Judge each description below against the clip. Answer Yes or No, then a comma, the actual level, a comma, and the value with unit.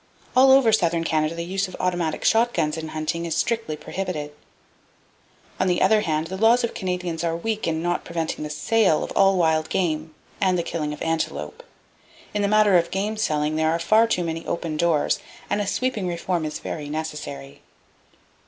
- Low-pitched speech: No, medium, 170 Hz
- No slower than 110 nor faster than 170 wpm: No, average, 190 wpm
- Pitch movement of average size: Yes, average, 3.8 semitones